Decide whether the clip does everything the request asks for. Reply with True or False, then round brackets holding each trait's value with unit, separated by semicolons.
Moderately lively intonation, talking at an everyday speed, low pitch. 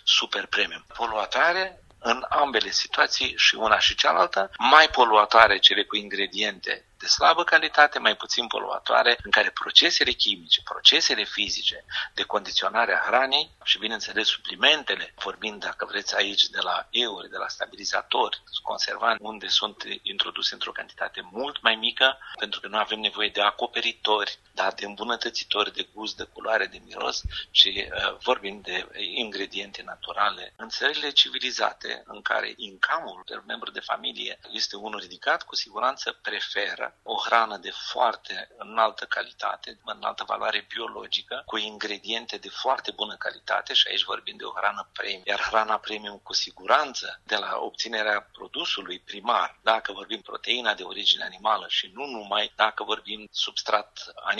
True (3.2 semitones; 150 wpm; 110 Hz)